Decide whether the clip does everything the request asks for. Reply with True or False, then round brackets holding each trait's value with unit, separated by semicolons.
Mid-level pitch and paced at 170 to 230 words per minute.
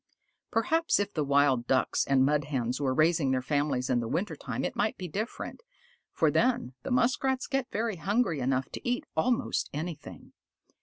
True (155 Hz; 175 wpm)